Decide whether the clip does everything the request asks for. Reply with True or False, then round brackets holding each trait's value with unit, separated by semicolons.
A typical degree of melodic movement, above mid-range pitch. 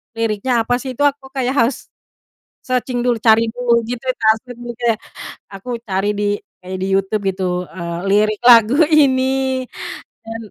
True (3.4 semitones; 235 Hz)